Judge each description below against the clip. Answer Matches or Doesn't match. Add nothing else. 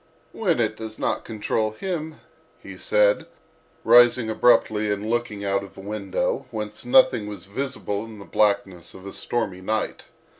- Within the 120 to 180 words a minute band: Matches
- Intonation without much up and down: Doesn't match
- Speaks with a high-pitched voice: Doesn't match